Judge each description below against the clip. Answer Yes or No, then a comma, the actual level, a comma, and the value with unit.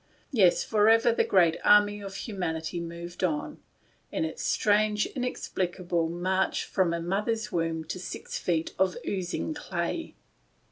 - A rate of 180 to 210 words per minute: No, average, 140 wpm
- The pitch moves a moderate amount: Yes, average, 3.6 semitones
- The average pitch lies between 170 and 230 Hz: Yes, medium, 185 Hz